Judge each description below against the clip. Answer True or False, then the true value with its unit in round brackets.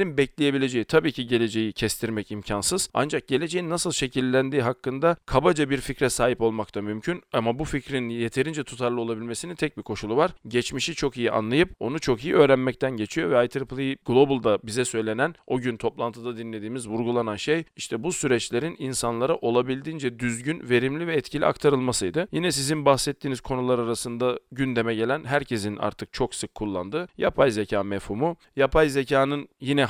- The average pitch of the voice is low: True (130 Hz)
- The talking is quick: True (150 wpm)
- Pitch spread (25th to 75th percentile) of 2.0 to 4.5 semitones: True (3.6 semitones)